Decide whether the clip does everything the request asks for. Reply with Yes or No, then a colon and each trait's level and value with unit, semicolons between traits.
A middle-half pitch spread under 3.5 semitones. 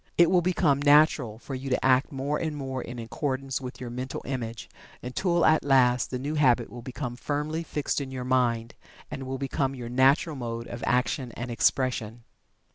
Yes: average, 2.8 semitones